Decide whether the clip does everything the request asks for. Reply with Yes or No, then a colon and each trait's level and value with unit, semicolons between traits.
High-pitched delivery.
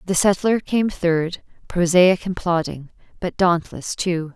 No: medium, 175 Hz